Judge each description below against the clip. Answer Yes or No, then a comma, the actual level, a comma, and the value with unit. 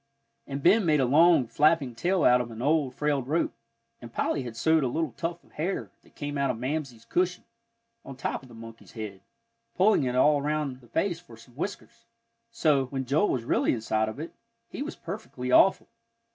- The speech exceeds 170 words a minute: Yes, average, 200 wpm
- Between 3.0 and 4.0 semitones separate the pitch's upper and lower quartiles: No, average, 4.8 semitones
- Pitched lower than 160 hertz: Yes, medium, 140 Hz